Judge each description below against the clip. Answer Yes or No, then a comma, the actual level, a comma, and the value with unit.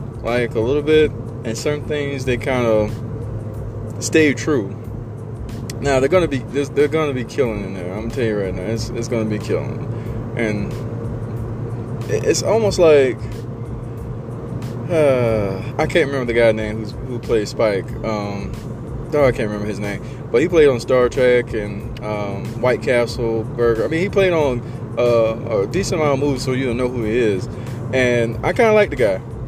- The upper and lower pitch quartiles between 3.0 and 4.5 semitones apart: No, narrow, 2.4 semitones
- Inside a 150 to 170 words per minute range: No, average, 185 wpm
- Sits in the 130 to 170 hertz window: No, low, 115 Hz